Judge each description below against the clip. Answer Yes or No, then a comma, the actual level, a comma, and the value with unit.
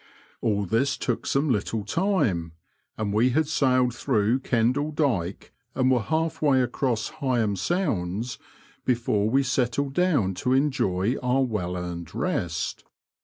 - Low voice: Yes, low, 125 Hz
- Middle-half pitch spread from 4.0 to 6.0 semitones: Yes, average, 5.1 semitones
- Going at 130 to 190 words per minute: Yes, slow, 135 wpm